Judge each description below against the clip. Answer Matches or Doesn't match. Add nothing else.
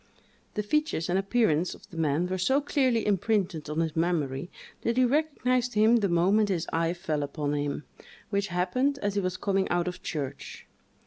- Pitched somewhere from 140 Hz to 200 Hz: Matches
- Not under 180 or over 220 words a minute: Matches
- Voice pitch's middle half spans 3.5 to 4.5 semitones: Doesn't match